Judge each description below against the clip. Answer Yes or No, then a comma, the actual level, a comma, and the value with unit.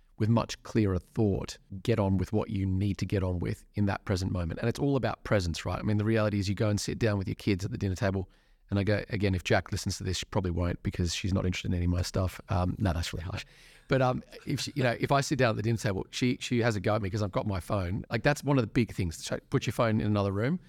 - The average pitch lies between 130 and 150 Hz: No, low, 105 Hz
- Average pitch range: Yes, average, 3.6 semitones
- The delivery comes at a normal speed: No, fast, 305 wpm